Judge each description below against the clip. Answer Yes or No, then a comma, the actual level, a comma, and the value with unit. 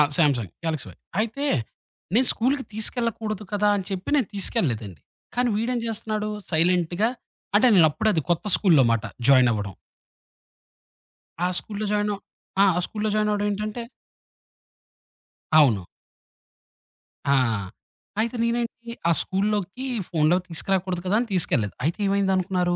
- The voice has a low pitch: No, high, 195 Hz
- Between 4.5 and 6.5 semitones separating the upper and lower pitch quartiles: Yes, average, 4.8 semitones